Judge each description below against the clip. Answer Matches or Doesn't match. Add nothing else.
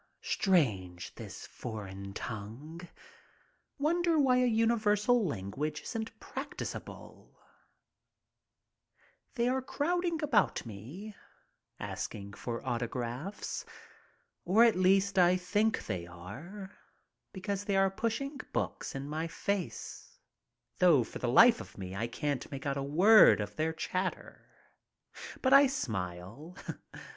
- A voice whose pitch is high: Doesn't match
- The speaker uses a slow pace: Matches